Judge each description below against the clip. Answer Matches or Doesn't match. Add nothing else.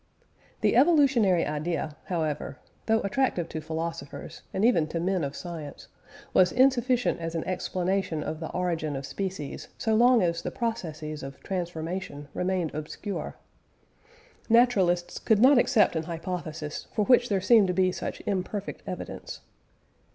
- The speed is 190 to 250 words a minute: Doesn't match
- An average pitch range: Matches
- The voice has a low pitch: Doesn't match